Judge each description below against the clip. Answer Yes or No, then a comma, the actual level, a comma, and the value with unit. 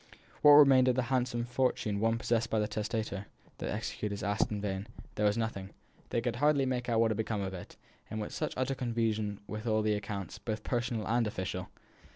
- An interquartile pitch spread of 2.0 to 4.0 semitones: Yes, narrow, 2.6 semitones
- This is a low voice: Yes, low, 110 Hz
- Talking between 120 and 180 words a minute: No, average, 200 wpm